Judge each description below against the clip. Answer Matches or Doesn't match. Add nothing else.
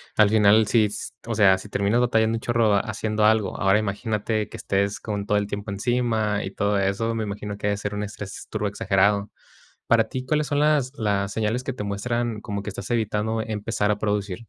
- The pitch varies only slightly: Matches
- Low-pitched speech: Matches